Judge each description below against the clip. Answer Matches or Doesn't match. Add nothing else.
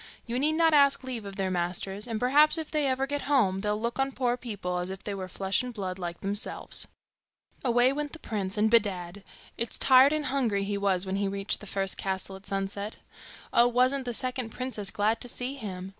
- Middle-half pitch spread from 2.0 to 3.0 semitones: Doesn't match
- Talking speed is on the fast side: Matches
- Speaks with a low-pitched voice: Doesn't match